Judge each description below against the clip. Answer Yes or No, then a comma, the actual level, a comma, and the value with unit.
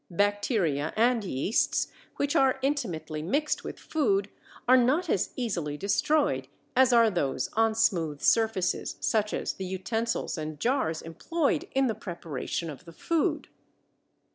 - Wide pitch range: Yes, wide, 7.4 semitones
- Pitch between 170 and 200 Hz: No, high, 210 Hz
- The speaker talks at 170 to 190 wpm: No, average, 140 wpm